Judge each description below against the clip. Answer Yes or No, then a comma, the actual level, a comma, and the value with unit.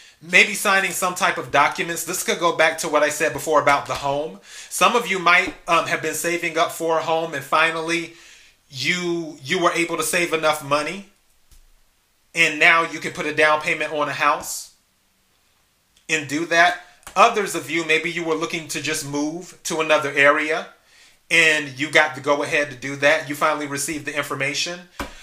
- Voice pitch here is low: No, medium, 160 Hz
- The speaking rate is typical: Yes, average, 195 wpm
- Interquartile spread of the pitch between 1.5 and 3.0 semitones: Yes, narrow, 2.5 semitones